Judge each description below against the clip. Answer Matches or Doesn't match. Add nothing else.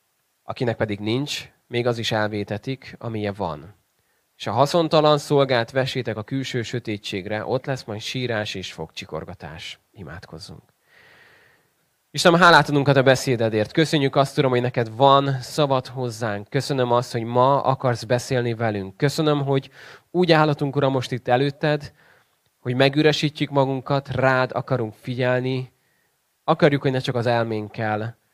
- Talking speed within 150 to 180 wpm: Doesn't match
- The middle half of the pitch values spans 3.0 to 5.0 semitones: Matches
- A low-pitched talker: Matches